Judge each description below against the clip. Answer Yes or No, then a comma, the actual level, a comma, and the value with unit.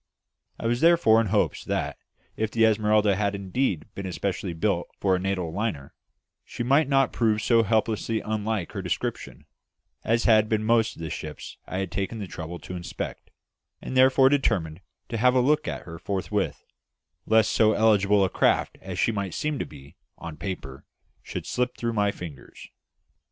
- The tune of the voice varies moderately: Yes, average, 3.8 semitones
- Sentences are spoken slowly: No, average, 180 wpm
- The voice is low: Yes, low, 105 Hz